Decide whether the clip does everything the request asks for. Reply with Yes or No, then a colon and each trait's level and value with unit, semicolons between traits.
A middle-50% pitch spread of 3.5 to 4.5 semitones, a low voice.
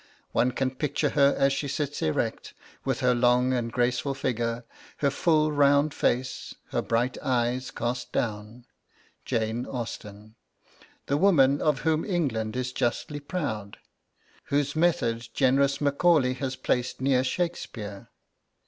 No: average, 3.0 semitones; low, 130 Hz